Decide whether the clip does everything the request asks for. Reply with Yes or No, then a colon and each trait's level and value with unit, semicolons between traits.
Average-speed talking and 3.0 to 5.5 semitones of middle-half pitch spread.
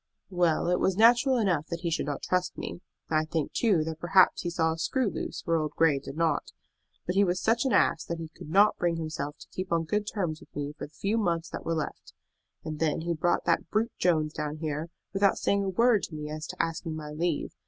No: fast, 245 wpm; average, 3.6 semitones